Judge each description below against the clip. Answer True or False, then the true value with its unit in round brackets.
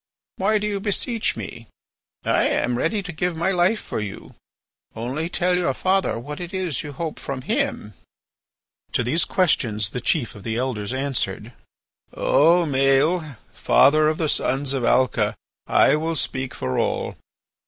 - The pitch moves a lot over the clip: True (6.1 semitones)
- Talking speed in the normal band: True (160 wpm)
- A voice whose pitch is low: False (150 Hz)